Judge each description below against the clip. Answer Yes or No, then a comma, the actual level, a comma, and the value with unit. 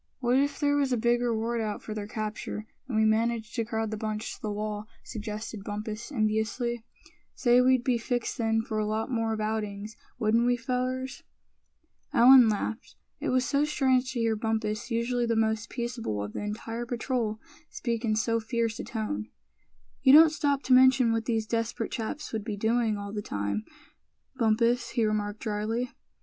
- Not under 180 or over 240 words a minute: Yes, average, 185 wpm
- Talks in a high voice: Yes, high, 225 Hz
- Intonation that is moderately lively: No, narrow, 2.2 semitones